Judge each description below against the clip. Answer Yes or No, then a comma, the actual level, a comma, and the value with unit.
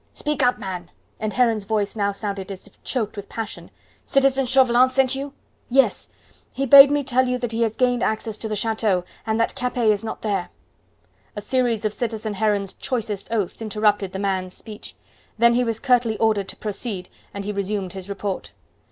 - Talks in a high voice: Yes, high, 220 Hz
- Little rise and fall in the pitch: No, average, 3.5 semitones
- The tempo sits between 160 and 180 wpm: No, average, 190 wpm